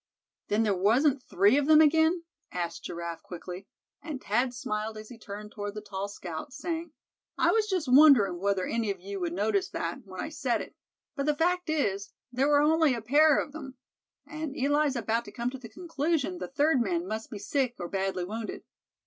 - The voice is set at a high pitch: Yes, high, 245 Hz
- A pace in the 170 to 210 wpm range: Yes, average, 200 wpm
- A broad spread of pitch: Yes, wide, 6.9 semitones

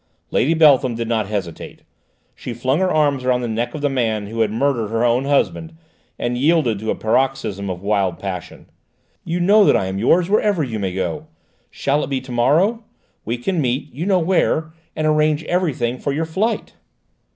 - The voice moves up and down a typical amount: No, wide, 5.9 semitones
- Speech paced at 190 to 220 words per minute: Yes, average, 195 wpm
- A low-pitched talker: Yes, low, 130 Hz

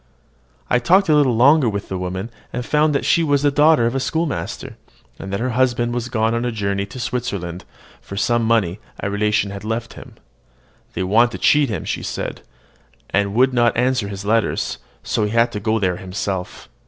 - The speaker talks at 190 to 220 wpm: Yes, average, 200 wpm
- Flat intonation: No, average, 4.2 semitones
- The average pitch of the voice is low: Yes, low, 115 Hz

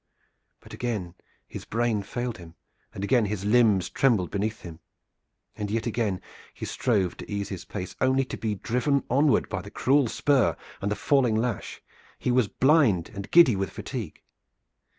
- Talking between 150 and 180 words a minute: Yes, average, 170 wpm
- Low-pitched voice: Yes, low, 110 Hz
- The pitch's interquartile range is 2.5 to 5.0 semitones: Yes, average, 4.1 semitones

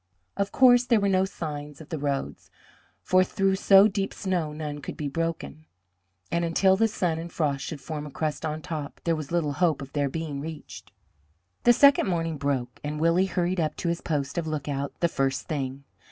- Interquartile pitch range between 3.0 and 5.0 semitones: Yes, average, 3.9 semitones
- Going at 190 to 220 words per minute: Yes, average, 200 wpm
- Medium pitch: Yes, medium, 160 Hz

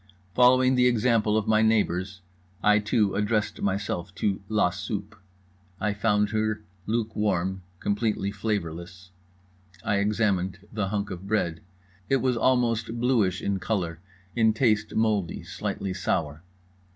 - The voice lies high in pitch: No, low, 105 Hz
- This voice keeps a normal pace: No, slow, 130 wpm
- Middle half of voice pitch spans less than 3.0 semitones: Yes, narrow, 2.5 semitones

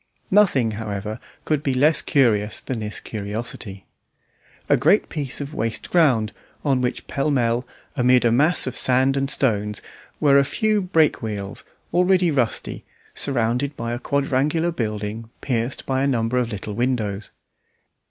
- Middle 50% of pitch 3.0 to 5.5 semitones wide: Yes, average, 4.2 semitones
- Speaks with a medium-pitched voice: No, low, 125 Hz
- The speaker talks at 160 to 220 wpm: No, average, 150 wpm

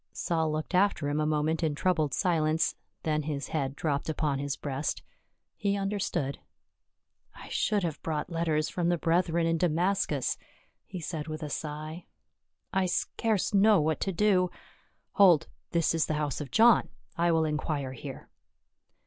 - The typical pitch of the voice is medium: Yes, medium, 160 Hz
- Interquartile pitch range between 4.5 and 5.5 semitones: No, average, 3.0 semitones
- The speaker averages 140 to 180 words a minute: Yes, average, 165 wpm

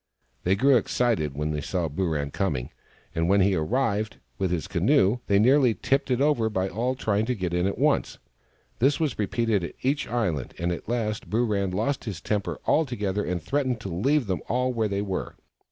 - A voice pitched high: No, low, 105 Hz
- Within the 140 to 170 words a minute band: No, average, 195 wpm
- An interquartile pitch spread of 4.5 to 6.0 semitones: Yes, average, 5.1 semitones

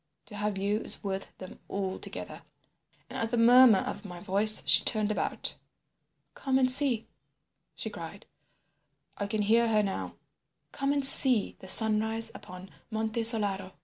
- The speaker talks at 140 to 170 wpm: Yes, average, 145 wpm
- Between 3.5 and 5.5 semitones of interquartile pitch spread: No, narrow, 2.6 semitones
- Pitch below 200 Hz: No, high, 215 Hz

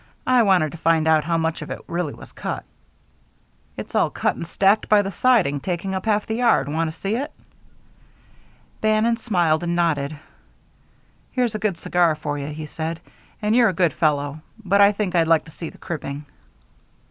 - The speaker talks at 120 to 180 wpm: No, average, 195 wpm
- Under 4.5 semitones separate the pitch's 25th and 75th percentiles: No, average, 4.8 semitones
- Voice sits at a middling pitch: Yes, medium, 170 Hz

